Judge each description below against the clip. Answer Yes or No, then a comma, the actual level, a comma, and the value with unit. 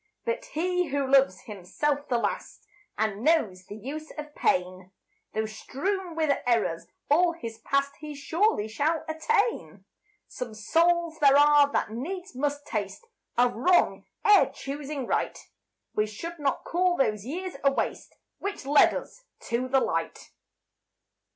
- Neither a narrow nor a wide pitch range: No, wide, 6.3 semitones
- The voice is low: No, very high, 285 Hz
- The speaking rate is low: No, average, 145 wpm